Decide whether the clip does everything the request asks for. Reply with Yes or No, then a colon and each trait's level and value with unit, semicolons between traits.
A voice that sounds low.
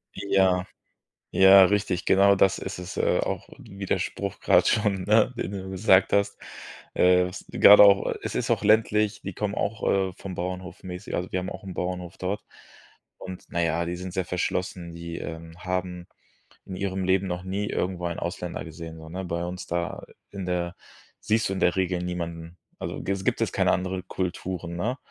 Yes: very low, 95 Hz